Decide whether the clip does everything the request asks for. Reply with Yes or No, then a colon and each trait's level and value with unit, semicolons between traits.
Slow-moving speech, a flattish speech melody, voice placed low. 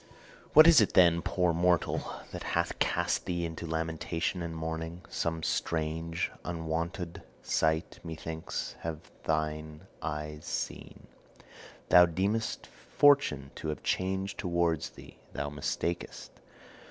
Yes: slow, 115 wpm; narrow, 1.8 semitones; very low, 80 Hz